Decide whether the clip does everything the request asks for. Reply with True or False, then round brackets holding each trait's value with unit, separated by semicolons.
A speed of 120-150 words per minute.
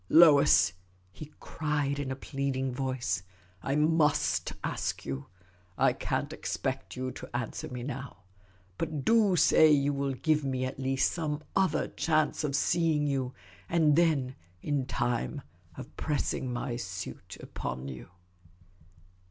True (145 wpm)